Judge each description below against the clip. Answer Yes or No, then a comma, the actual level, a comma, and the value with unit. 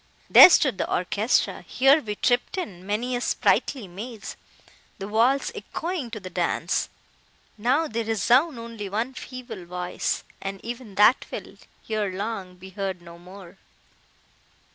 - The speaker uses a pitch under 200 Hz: No, high, 220 Hz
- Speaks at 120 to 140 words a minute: Yes, slow, 135 wpm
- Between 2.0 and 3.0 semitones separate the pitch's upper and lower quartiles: No, average, 4.4 semitones